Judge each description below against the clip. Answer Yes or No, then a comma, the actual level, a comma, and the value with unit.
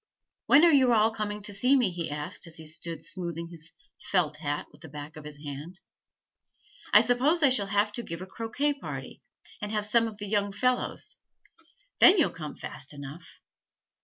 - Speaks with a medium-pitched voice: No, high, 200 Hz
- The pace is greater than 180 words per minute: Yes, average, 190 wpm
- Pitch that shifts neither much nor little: No, wide, 6.3 semitones